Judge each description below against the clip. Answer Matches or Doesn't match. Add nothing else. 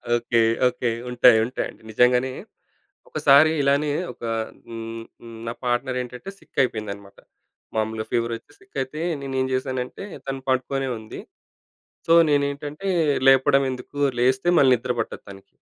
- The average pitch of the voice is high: Doesn't match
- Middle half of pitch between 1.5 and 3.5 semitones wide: Matches